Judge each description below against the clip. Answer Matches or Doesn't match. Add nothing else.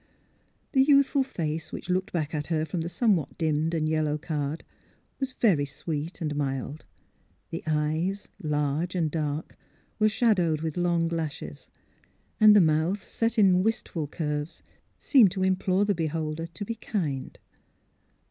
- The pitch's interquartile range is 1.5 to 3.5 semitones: Doesn't match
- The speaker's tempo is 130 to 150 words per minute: Matches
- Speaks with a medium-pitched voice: Matches